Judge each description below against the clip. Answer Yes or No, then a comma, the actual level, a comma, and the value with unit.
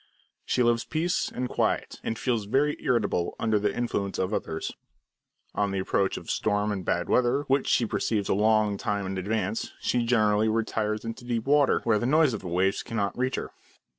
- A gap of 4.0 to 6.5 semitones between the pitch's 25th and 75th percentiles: No, average, 3.1 semitones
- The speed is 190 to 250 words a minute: Yes, average, 195 wpm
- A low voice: Yes, low, 110 Hz